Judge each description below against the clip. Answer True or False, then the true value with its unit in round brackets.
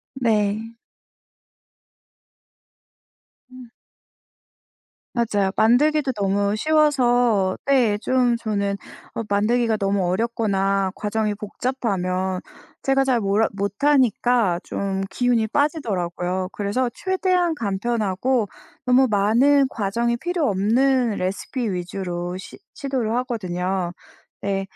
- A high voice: True (220 Hz)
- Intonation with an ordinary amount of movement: True (4.4 semitones)